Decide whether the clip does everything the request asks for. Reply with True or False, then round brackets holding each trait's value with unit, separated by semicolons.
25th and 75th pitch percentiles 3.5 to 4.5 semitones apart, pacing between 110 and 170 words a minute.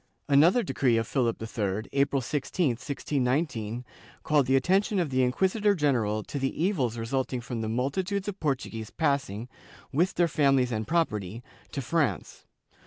False (5.4 semitones; 155 wpm)